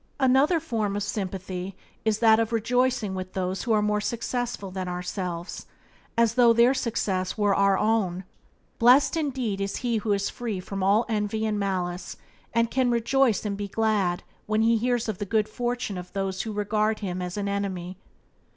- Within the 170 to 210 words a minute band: Yes, average, 180 wpm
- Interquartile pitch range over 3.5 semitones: No, average, 3.2 semitones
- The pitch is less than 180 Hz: No, high, 210 Hz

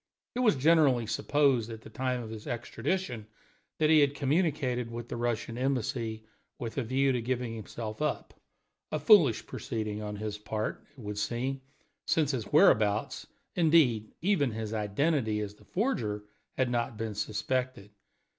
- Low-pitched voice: Yes, low, 120 Hz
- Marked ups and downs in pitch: No, average, 4.1 semitones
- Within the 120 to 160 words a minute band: Yes, average, 155 wpm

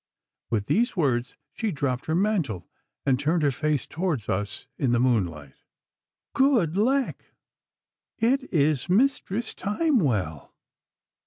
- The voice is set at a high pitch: No, medium, 155 Hz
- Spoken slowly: Yes, slow, 115 wpm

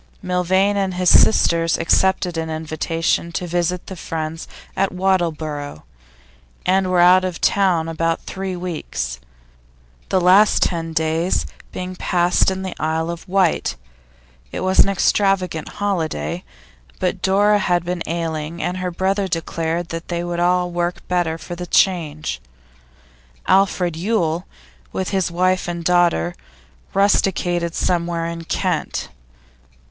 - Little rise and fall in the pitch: Yes, narrow, 2.1 semitones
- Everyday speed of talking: No, slow, 130 wpm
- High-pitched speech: No, medium, 175 Hz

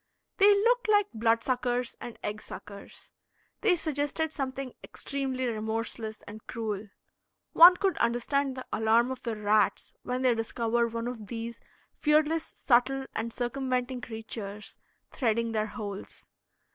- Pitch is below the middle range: No, high, 240 Hz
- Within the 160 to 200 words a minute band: No, slow, 135 wpm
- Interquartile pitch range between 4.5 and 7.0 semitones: No, average, 3.5 semitones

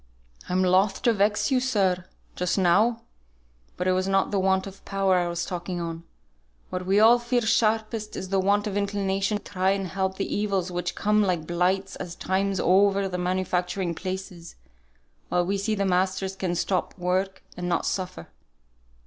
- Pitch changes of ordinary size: No, narrow, 1.8 semitones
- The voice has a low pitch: No, high, 190 Hz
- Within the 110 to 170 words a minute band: No, average, 180 wpm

